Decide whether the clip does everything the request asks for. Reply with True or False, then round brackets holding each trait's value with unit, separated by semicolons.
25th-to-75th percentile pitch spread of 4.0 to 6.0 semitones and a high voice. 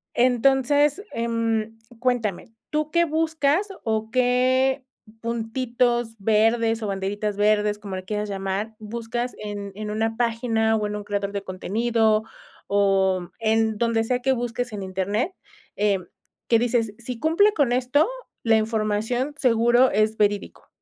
False (3.0 semitones; 225 Hz)